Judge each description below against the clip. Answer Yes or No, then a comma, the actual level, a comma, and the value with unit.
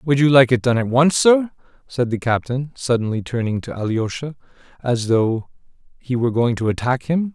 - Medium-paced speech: Yes, average, 190 wpm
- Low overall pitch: Yes, low, 125 Hz